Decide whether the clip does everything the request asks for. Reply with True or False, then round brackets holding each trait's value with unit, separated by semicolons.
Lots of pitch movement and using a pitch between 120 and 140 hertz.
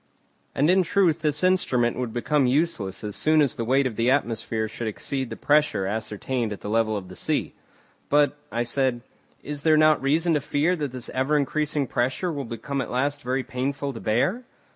False (4.1 semitones; 135 Hz)